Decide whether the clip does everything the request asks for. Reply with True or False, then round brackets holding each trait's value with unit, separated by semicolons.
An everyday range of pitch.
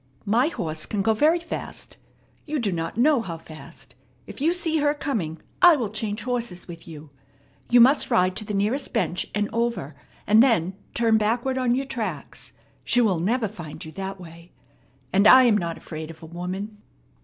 False (5.9 semitones)